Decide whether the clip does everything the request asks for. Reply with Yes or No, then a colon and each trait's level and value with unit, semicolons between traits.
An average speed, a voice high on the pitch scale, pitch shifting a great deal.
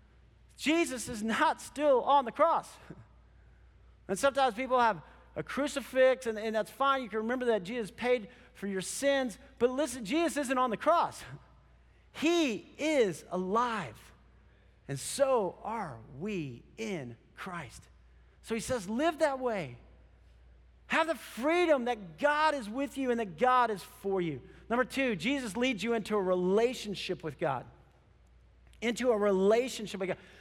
Yes: average, 150 wpm; high, 230 Hz; wide, 6.3 semitones